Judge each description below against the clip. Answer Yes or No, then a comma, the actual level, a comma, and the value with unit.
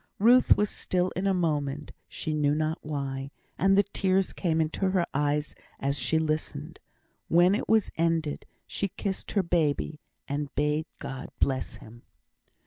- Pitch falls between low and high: Yes, medium, 155 Hz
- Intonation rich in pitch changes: No, average, 4.3 semitones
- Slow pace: No, average, 155 wpm